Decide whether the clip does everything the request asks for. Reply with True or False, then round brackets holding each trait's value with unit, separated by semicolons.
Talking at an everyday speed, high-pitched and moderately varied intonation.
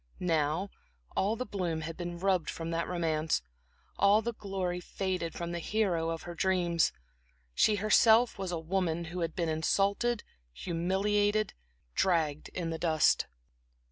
False (145 wpm; 175 Hz; 3.1 semitones)